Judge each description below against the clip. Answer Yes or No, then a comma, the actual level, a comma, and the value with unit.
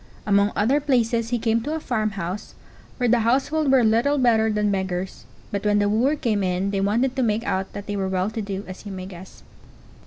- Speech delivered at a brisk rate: Yes, fast, 220 wpm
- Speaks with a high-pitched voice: Yes, high, 215 Hz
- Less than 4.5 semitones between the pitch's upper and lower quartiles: Yes, average, 3.5 semitones